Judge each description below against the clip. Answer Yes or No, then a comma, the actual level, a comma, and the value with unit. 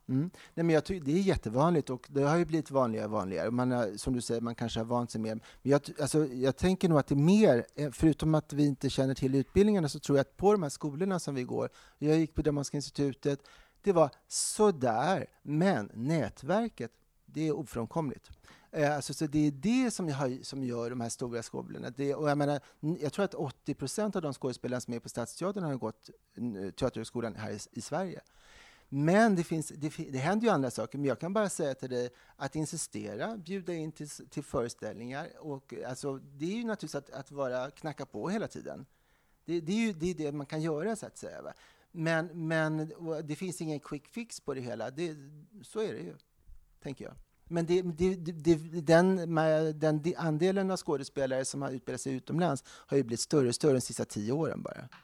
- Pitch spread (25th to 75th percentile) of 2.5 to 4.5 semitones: Yes, average, 4.2 semitones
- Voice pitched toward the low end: No, medium, 150 Hz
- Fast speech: Yes, fast, 215 wpm